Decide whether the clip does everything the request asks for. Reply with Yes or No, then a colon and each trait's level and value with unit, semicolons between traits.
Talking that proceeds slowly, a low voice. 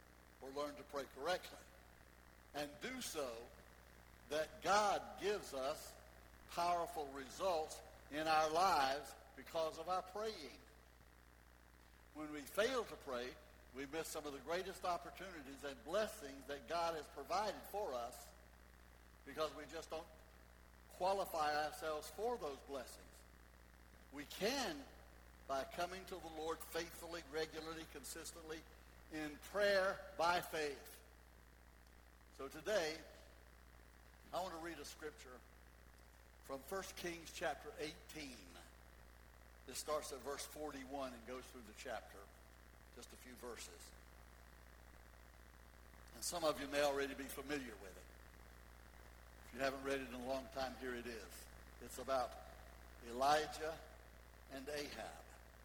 Yes: slow, 125 wpm; low, 125 Hz